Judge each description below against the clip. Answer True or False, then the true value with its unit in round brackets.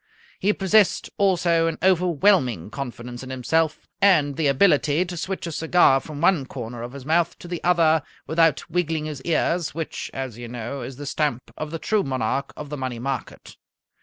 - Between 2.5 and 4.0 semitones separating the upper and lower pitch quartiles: False (4.5 semitones)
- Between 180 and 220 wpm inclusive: True (185 wpm)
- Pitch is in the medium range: True (150 Hz)